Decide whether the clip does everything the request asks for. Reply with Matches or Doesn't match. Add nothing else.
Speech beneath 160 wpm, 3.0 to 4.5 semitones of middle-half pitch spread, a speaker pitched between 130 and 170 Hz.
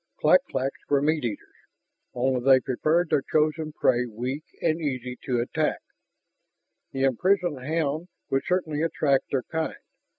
Matches